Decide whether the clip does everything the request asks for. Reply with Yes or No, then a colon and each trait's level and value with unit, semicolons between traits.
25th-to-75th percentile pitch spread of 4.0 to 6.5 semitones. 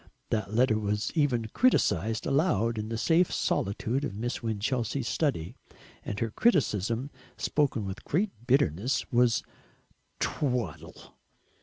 Yes: average, 4.4 semitones